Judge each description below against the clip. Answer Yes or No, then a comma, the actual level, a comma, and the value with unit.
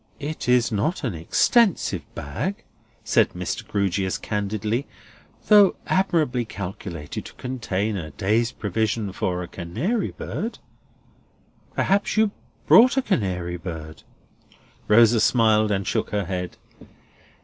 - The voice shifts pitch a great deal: Yes, wide, 6.0 semitones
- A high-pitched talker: No, low, 105 Hz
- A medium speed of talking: No, slow, 115 wpm